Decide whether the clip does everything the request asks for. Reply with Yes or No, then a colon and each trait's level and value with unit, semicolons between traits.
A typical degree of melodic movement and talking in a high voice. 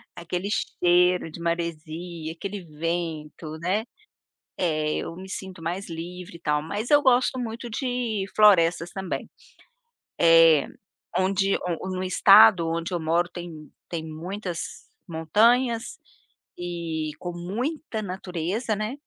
No: average, 3.7 semitones; medium, 175 Hz